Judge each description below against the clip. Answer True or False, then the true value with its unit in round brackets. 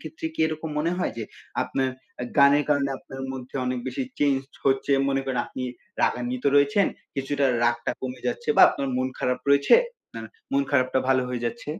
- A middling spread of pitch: False (2.1 semitones)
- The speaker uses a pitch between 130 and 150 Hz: True (135 Hz)